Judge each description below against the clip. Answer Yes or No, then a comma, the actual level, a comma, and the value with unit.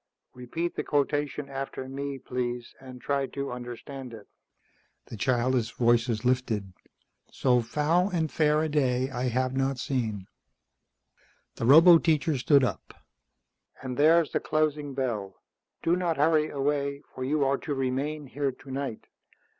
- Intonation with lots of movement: No, average, 2.9 semitones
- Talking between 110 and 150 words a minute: Yes, average, 140 wpm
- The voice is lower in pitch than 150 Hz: Yes, low, 135 Hz